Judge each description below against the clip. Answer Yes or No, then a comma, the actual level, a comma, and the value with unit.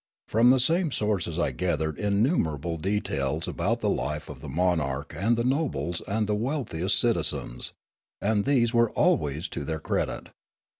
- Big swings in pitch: Yes, wide, 6.9 semitones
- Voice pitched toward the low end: Yes, low, 100 Hz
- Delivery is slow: No, average, 160 wpm